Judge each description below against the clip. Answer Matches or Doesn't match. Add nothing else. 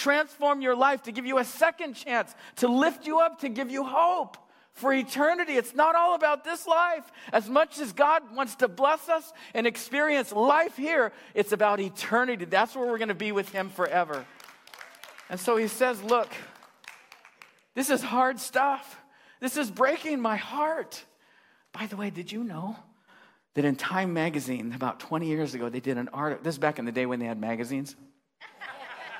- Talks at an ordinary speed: Matches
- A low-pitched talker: Doesn't match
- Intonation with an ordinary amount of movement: Doesn't match